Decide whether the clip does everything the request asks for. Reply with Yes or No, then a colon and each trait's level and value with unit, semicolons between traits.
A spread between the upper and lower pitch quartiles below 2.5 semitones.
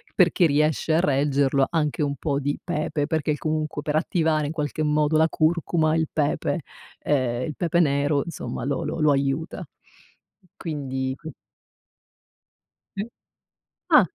Yes: narrow, 2.1 semitones